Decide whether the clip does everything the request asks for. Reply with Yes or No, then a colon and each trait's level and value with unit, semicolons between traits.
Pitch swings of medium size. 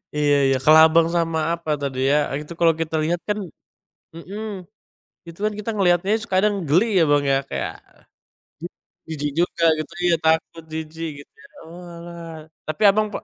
No: narrow, 2.0 semitones